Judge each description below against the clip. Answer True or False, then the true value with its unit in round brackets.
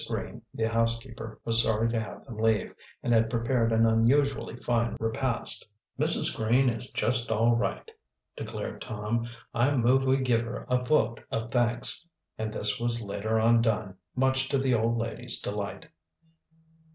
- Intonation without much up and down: True (1.8 semitones)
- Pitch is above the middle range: False (115 Hz)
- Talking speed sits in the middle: True (160 wpm)